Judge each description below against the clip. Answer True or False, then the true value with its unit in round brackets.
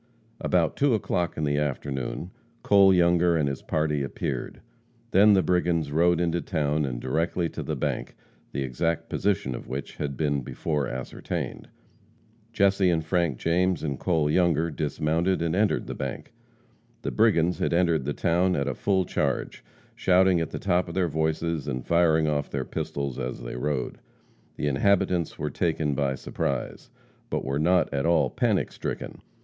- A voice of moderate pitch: False (80 Hz)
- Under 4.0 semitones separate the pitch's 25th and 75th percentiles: True (3.5 semitones)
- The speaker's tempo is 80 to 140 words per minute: False (165 wpm)